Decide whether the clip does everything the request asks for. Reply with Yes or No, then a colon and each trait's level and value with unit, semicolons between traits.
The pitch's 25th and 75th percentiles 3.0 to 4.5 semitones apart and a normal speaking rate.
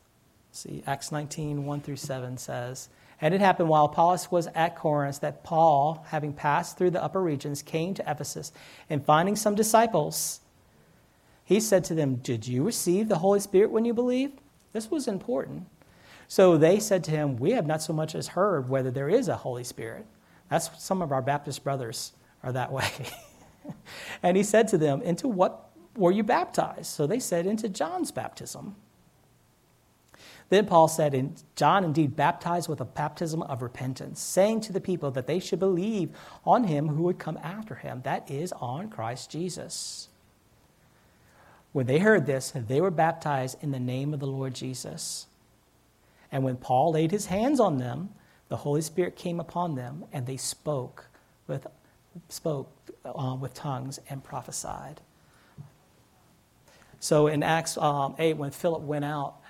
No: average, 4.9 semitones; average, 170 wpm